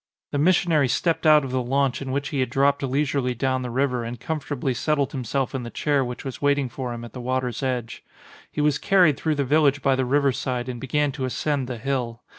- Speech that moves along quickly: Yes, fast, 240 wpm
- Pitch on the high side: No, low, 135 Hz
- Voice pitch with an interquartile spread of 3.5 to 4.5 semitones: No, narrow, 2.4 semitones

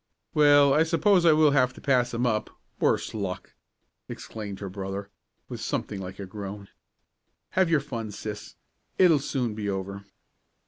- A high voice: No, low, 115 Hz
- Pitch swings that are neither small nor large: No, wide, 6.3 semitones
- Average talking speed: Yes, average, 155 wpm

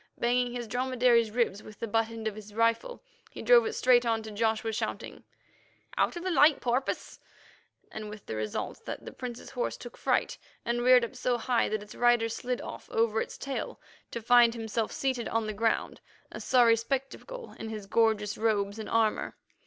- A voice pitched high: Yes, high, 230 Hz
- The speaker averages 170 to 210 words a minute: Yes, average, 190 wpm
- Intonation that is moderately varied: No, narrow, 2.2 semitones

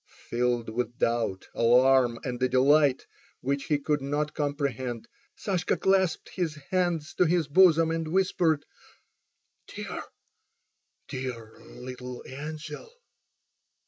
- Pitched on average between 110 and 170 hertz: Yes, medium, 140 Hz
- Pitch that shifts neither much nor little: Yes, average, 4.3 semitones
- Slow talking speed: Yes, slow, 105 wpm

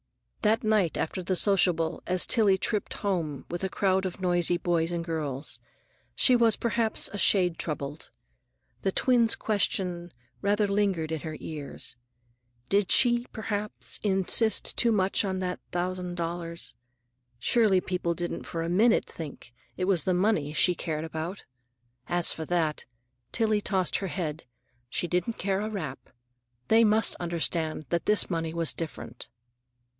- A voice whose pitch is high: No, medium, 180 Hz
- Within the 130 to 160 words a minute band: Yes, average, 150 wpm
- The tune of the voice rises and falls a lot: No, average, 3.6 semitones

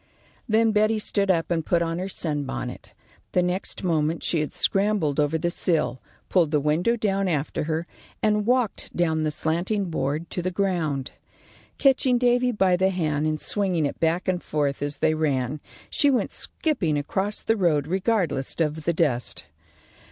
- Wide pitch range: No, average, 4.6 semitones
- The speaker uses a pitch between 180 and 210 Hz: No, medium, 170 Hz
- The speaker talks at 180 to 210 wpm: No, average, 170 wpm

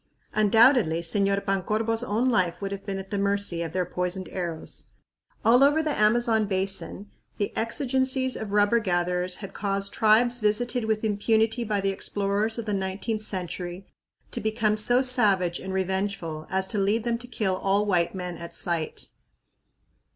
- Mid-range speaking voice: No, high, 205 Hz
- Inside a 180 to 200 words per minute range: No, average, 165 wpm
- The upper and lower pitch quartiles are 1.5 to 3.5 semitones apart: Yes, average, 2.9 semitones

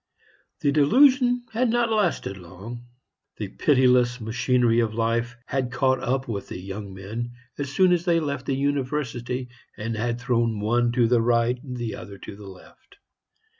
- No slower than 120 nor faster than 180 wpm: Yes, average, 160 wpm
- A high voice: No, low, 120 Hz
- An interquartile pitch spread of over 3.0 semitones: Yes, average, 3.6 semitones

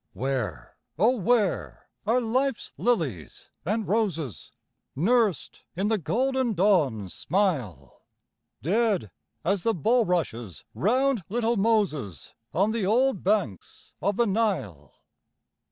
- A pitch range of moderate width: No, wide, 8.1 semitones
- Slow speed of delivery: Yes, slow, 105 wpm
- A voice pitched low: No, high, 200 Hz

